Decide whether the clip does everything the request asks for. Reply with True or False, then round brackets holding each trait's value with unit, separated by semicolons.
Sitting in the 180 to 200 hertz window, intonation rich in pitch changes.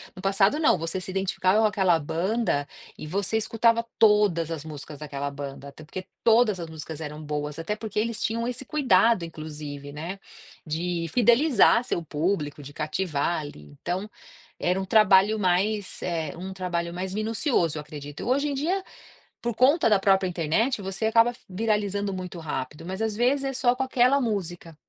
True (190 Hz; 5.7 semitones)